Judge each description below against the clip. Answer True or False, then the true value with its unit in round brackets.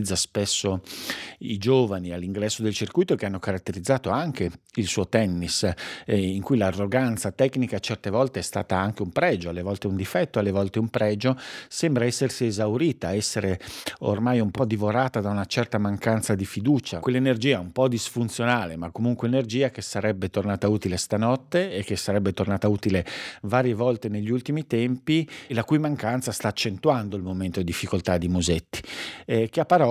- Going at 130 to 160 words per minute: False (170 wpm)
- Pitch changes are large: False (4.1 semitones)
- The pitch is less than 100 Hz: False (105 Hz)